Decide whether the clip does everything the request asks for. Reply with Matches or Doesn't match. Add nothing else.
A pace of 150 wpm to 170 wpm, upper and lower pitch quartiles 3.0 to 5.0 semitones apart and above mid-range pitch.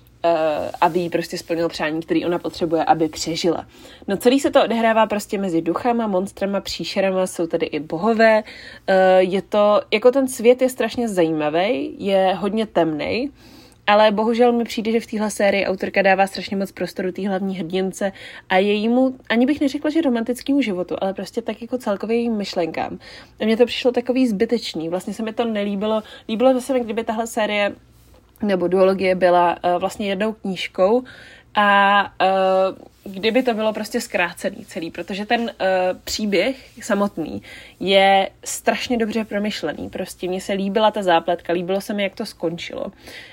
Matches